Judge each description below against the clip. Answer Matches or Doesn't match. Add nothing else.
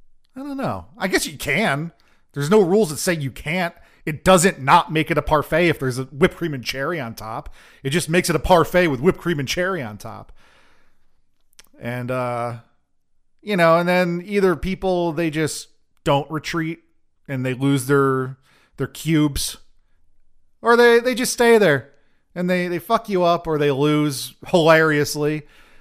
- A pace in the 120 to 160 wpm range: Doesn't match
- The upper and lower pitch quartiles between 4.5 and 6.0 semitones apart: Matches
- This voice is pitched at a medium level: Matches